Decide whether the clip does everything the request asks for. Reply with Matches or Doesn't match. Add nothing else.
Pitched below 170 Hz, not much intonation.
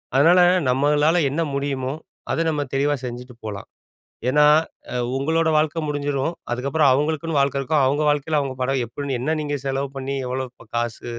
Matches